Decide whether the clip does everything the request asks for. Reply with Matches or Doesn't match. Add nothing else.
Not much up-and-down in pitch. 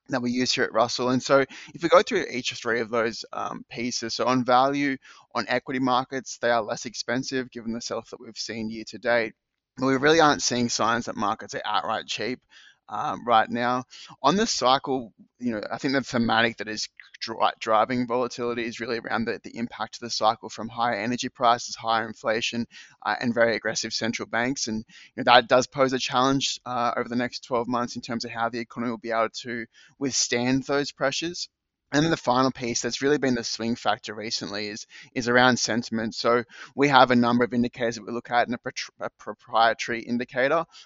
Matches